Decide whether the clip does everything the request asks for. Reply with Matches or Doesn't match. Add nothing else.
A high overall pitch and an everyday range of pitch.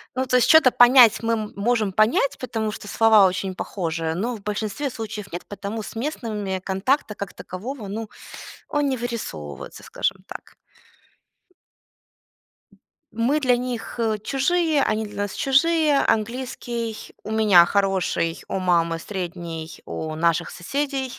Matches